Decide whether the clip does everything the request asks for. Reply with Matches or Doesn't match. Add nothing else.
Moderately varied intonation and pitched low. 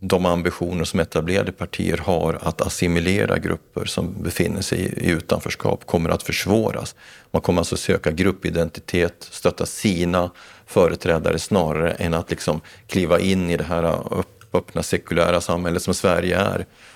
Doesn't match